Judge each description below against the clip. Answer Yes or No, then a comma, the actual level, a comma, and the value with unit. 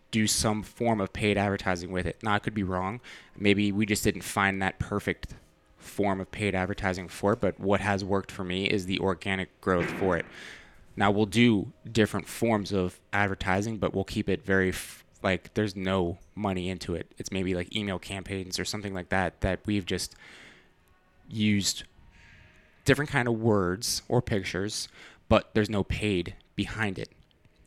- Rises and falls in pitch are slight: Yes, narrow, 2.2 semitones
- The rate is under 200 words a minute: Yes, average, 180 wpm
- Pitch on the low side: Yes, low, 100 Hz